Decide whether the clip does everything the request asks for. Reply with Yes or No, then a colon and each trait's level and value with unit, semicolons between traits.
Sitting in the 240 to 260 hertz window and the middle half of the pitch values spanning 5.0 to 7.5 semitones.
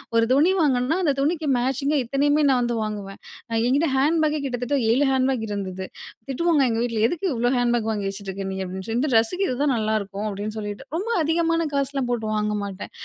Yes: high, 245 Hz; wide, 5.4 semitones